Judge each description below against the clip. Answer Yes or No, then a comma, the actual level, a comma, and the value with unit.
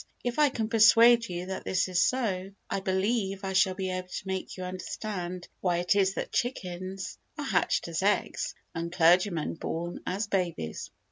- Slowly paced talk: No, average, 180 wpm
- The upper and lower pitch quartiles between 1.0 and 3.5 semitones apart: Yes, narrow, 2.4 semitones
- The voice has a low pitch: No, high, 190 Hz